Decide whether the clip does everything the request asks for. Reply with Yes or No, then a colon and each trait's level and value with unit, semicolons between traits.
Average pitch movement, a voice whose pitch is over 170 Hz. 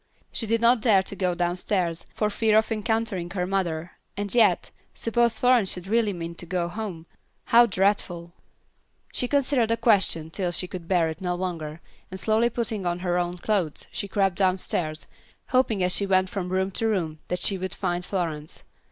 Yes: average, 3.8 semitones; high, 190 Hz